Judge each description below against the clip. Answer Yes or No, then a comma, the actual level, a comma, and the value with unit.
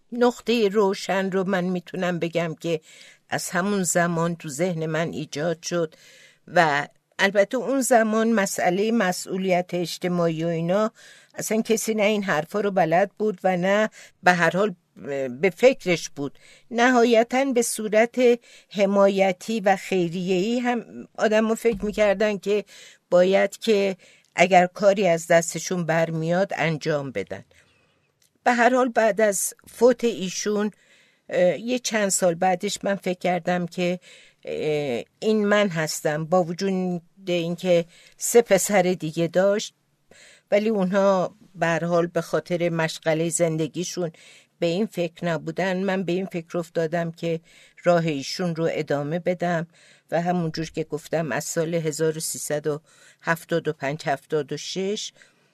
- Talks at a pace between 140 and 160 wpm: No, average, 125 wpm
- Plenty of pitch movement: No, average, 3.7 semitones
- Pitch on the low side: No, medium, 180 Hz